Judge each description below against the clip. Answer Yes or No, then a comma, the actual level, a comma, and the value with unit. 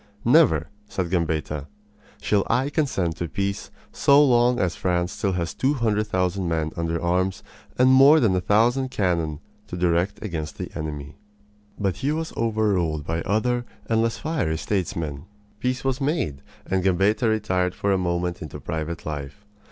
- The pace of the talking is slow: No, average, 160 wpm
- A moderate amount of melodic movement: No, wide, 5.7 semitones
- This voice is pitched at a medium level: No, very low, 95 Hz